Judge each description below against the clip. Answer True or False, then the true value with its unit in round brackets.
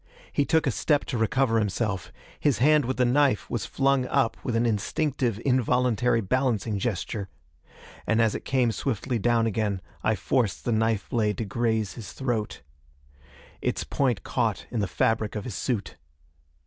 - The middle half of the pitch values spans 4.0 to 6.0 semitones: False (3.2 semitones)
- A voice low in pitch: True (115 Hz)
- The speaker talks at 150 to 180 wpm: True (165 wpm)